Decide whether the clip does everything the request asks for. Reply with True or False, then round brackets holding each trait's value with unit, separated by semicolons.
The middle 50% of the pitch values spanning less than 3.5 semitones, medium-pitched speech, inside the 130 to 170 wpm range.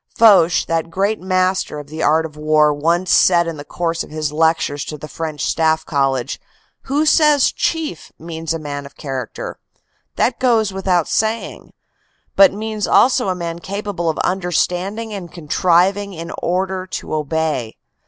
False (4.0 semitones; 170 Hz; 160 wpm)